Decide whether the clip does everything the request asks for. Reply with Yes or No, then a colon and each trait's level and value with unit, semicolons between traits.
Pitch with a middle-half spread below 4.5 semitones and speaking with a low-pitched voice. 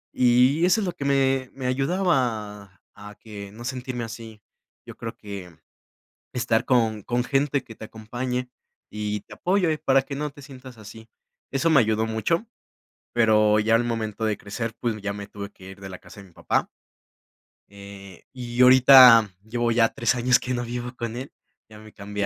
Yes: average, 3.4 semitones; low, 115 Hz